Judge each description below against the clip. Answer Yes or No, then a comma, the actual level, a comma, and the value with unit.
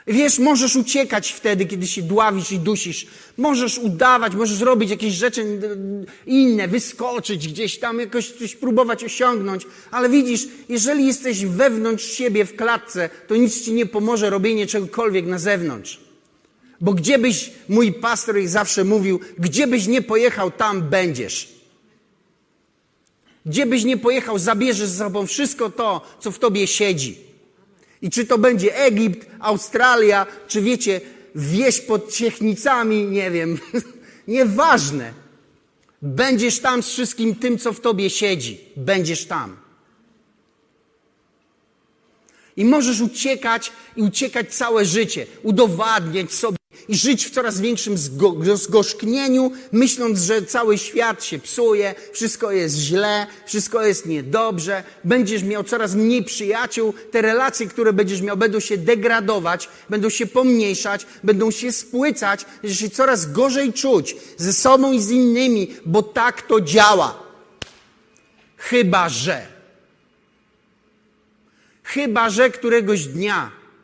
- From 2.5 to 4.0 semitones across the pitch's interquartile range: Yes, average, 3.3 semitones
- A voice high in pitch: Yes, high, 220 Hz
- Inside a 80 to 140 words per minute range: Yes, average, 130 wpm